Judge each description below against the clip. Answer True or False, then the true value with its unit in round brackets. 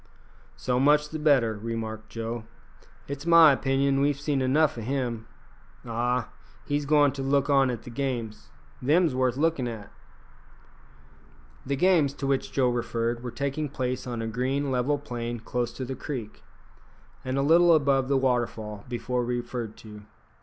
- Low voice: True (130 Hz)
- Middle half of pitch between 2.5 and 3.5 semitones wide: True (3.0 semitones)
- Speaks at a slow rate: False (160 wpm)